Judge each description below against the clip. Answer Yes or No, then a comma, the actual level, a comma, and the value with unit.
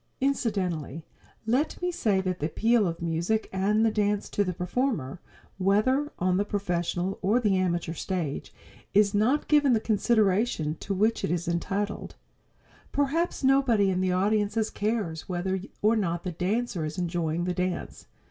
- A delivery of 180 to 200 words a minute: No, average, 155 wpm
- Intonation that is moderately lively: Yes, average, 4.0 semitones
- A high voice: Yes, high, 195 Hz